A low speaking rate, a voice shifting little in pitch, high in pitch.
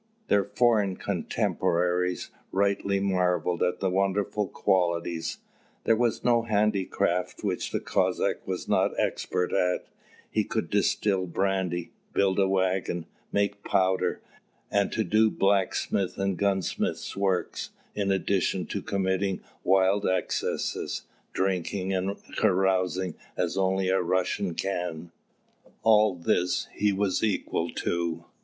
No: slow, 115 wpm; narrow, 1.7 semitones; very low, 95 Hz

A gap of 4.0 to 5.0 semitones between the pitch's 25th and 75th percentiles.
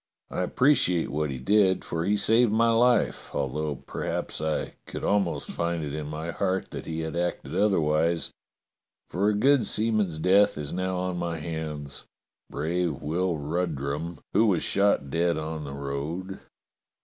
Yes: average, 4.3 semitones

